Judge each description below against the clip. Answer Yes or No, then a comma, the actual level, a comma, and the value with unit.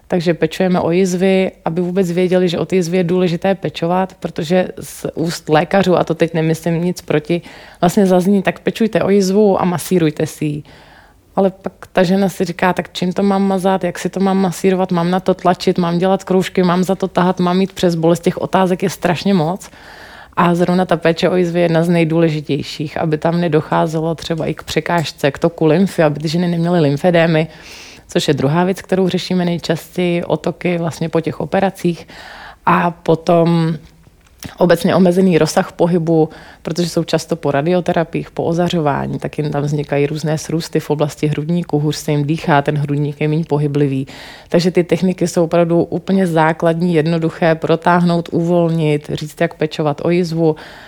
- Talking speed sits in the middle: No, fast, 180 wpm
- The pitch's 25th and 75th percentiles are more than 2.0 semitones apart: Yes, narrow, 2.4 semitones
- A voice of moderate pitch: Yes, medium, 170 Hz